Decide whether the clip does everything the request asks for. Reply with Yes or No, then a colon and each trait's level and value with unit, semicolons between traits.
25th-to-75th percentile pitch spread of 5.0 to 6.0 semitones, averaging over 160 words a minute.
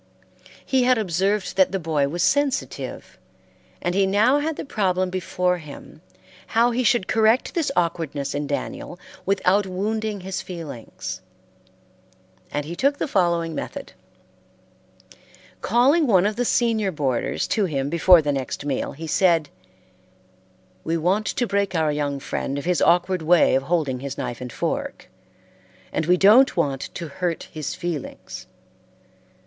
No: average, 5.3 semitones; average, 150 wpm